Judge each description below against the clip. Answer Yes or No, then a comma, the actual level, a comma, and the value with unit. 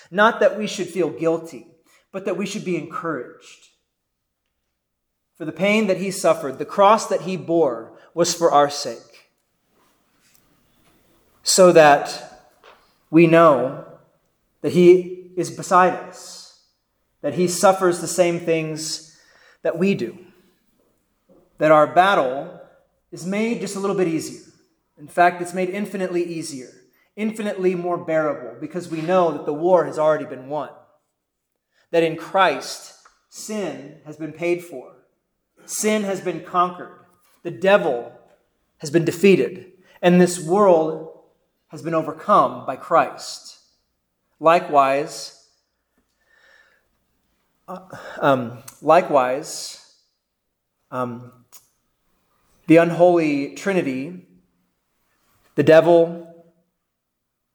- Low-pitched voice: No, medium, 170 Hz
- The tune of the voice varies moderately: Yes, average, 3.0 semitones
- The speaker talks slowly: Yes, slow, 115 wpm